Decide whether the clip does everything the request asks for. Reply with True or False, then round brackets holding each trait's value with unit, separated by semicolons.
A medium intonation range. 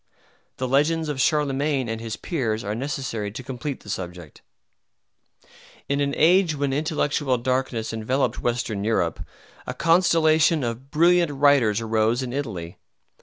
True (4.7 semitones)